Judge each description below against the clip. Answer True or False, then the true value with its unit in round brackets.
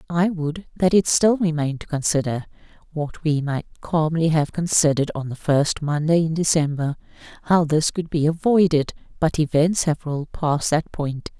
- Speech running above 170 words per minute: False (165 wpm)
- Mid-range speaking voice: True (155 Hz)